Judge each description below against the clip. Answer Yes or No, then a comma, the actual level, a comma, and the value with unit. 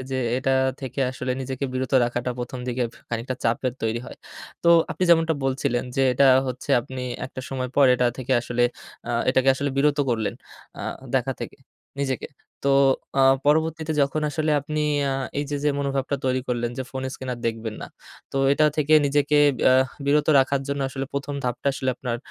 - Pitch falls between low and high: No, low, 130 Hz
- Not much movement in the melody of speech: Yes, narrow, 2.1 semitones